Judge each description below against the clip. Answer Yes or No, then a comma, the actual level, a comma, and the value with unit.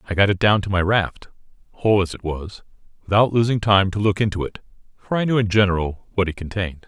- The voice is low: Yes, low, 100 Hz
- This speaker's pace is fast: Yes, fast, 225 wpm